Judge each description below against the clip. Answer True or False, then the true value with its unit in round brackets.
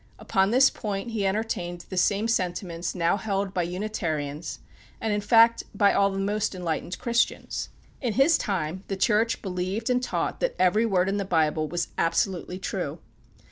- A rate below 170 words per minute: False (175 wpm)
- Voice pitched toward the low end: False (195 Hz)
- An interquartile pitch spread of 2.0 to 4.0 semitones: True (3.5 semitones)